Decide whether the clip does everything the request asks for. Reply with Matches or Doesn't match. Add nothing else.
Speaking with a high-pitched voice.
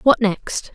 Matches